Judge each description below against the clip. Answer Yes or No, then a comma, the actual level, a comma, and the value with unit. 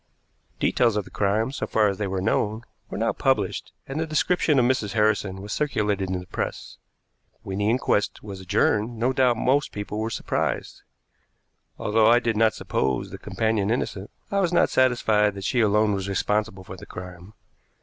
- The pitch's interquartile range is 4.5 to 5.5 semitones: No, average, 3.3 semitones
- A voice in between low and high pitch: No, low, 105 Hz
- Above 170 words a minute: Yes, average, 185 wpm